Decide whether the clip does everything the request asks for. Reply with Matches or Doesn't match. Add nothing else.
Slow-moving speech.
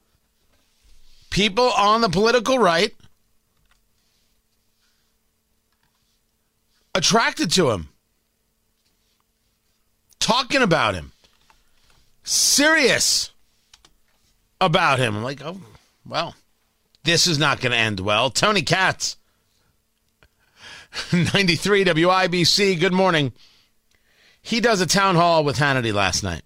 Matches